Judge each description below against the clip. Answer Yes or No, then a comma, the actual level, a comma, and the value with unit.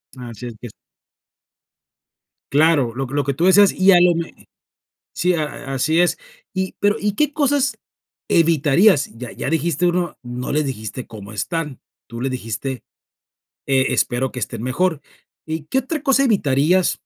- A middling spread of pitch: No, wide, 5.9 semitones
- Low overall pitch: No, medium, 150 Hz